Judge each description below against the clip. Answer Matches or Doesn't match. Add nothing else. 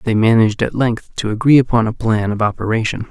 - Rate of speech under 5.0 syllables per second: Doesn't match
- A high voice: Doesn't match